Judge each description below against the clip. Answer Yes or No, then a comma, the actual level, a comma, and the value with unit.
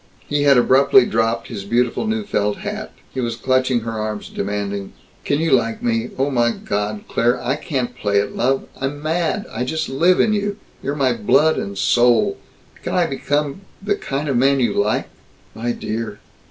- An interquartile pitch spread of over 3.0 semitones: Yes, average, 4.2 semitones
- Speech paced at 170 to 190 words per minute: Yes, average, 185 wpm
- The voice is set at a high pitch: No, low, 125 Hz